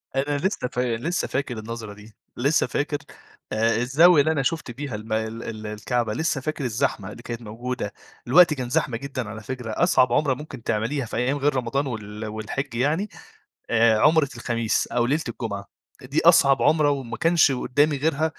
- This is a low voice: Yes, low, 125 Hz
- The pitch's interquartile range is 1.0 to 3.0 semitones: No, average, 4.3 semitones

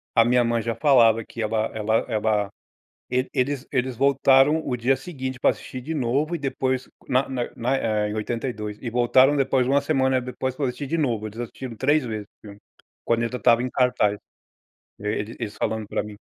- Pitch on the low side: Yes, low, 125 Hz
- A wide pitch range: No, average, 3.1 semitones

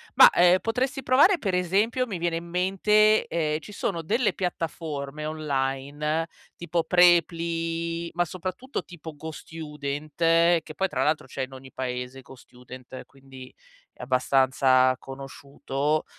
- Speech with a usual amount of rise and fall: Yes, average, 4.5 semitones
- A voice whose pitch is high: No, medium, 160 Hz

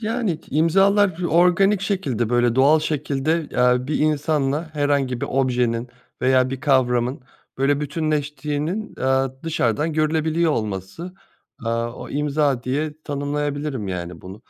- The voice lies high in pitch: No, medium, 145 Hz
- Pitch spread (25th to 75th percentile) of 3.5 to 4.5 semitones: Yes, average, 3.9 semitones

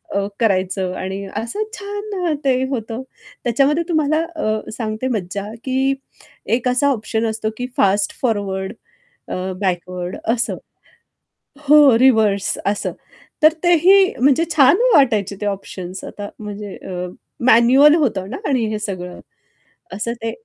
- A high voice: Yes, high, 225 Hz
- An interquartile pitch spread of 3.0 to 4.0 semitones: No, wide, 5.4 semitones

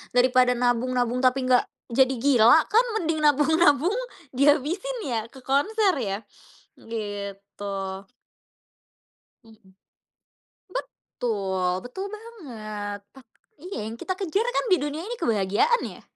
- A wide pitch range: Yes, wide, 7.2 semitones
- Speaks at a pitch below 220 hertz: No, very high, 255 Hz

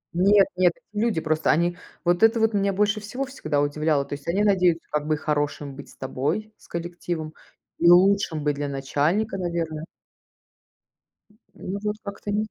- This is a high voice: No, medium, 175 Hz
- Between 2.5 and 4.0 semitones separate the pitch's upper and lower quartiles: No, average, 5.0 semitones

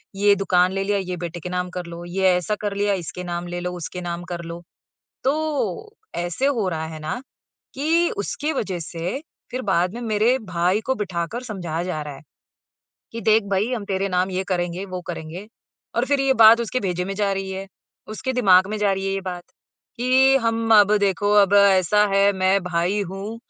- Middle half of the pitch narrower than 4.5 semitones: Yes, average, 3.1 semitones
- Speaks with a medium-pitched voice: No, high, 195 Hz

